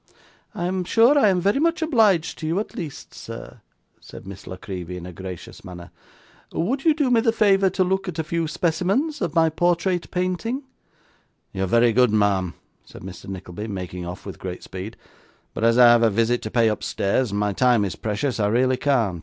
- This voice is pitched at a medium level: No, low, 125 Hz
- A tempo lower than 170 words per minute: No, fast, 205 wpm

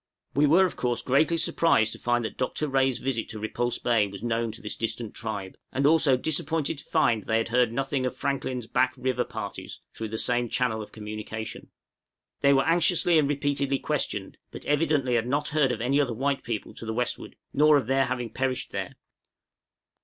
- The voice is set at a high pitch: No, low, 125 Hz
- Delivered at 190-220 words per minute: Yes, average, 200 wpm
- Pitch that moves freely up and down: No, average, 3.8 semitones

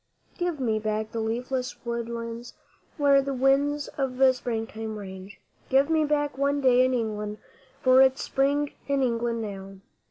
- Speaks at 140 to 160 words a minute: Yes, average, 150 wpm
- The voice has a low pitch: No, very high, 250 Hz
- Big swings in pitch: No, average, 3.7 semitones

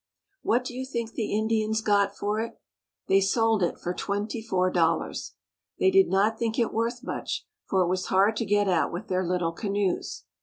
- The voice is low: No, high, 205 Hz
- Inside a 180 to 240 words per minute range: Yes, average, 200 wpm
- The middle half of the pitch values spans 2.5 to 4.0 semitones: Yes, average, 3.2 semitones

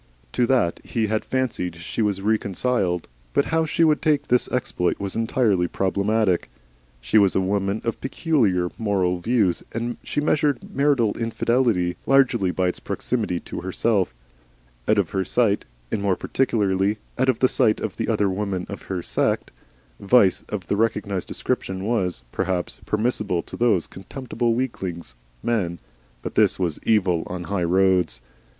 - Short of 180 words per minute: Yes, average, 160 wpm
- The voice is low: Yes, low, 100 Hz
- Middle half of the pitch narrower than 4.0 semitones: No, average, 4.4 semitones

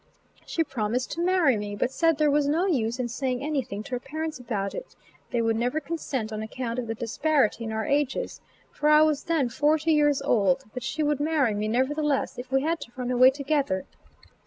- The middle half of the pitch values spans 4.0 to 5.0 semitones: Yes, average, 4.5 semitones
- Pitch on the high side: Yes, very high, 265 Hz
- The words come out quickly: Yes, fast, 210 wpm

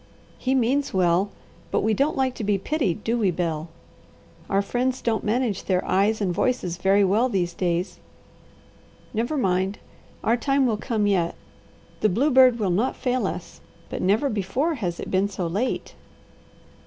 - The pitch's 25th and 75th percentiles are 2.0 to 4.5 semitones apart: No, average, 5.1 semitones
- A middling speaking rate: Yes, average, 165 wpm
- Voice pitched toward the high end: Yes, high, 210 Hz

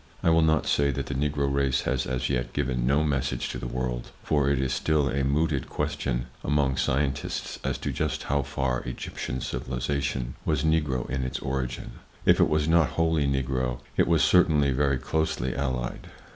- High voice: No, very low, 70 Hz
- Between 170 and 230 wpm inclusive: Yes, average, 185 wpm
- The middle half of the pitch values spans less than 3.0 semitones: Yes, narrow, 2.4 semitones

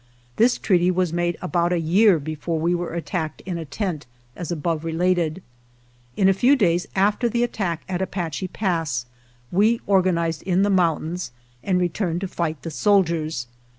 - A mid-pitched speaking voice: Yes, medium, 175 Hz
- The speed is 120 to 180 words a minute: Yes, average, 175 wpm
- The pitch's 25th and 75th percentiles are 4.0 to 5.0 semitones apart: No, average, 2.7 semitones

